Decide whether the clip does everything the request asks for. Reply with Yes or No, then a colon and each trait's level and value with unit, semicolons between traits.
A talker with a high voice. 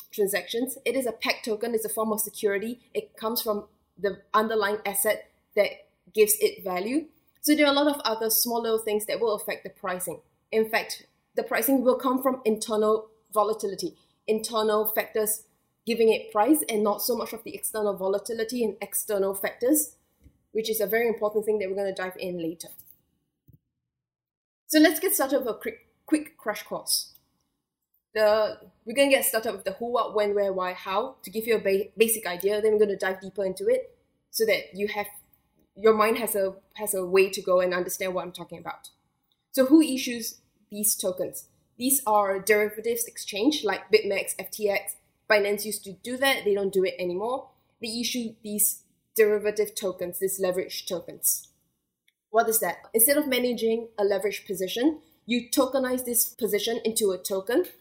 Yes: high, 215 Hz